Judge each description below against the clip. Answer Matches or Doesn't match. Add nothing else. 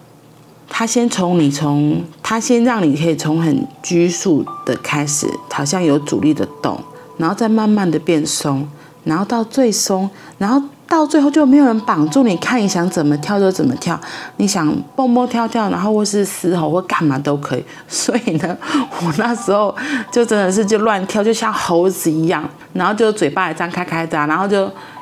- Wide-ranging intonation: Matches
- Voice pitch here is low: Doesn't match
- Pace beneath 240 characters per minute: Doesn't match